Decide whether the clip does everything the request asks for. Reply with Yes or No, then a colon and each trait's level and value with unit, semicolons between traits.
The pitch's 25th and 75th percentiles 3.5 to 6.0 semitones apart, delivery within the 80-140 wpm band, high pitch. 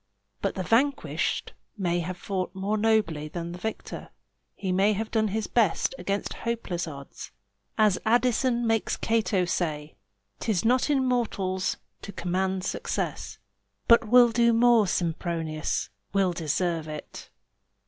Yes: average, 4.5 semitones; slow, 135 wpm; high, 195 Hz